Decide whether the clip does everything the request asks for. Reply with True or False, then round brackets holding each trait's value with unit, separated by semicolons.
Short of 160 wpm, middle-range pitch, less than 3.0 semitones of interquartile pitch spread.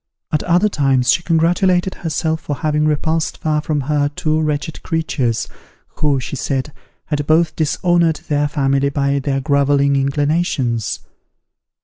True (135 wpm; 150 Hz; 2.5 semitones)